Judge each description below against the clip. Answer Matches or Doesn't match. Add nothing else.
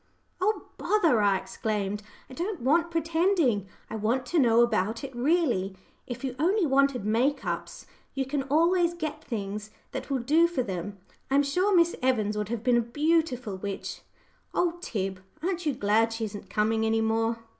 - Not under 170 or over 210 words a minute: Matches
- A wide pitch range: Matches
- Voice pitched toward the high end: Matches